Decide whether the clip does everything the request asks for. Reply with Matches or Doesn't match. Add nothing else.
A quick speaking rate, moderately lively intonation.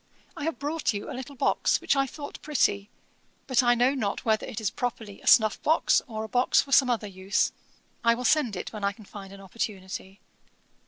Matches